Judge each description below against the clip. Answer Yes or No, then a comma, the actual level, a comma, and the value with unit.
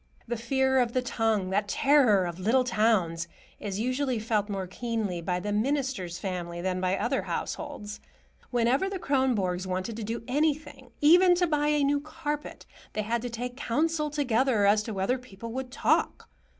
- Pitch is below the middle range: No, high, 235 Hz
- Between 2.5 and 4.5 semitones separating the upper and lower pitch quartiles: No, wide, 5.6 semitones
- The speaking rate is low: No, average, 175 wpm